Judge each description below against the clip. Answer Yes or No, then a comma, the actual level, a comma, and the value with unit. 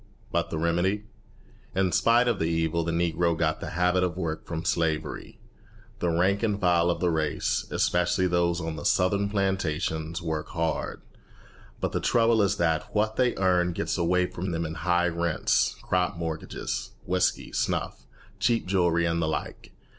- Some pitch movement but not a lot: No, narrow, 2.2 semitones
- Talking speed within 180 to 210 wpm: No, average, 170 wpm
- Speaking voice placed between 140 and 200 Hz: No, very low, 85 Hz